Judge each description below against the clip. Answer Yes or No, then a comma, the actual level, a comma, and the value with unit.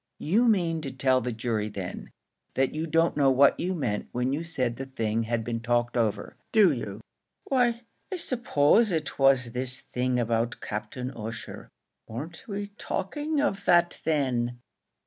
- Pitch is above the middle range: No, low, 130 Hz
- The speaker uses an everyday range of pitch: No, wide, 6.2 semitones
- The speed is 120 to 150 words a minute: No, average, 165 wpm